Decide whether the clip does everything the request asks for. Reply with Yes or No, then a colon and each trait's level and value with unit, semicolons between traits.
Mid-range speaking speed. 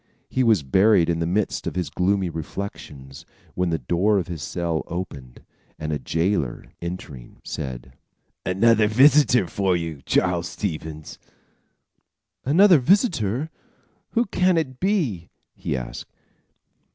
No: slow, 125 wpm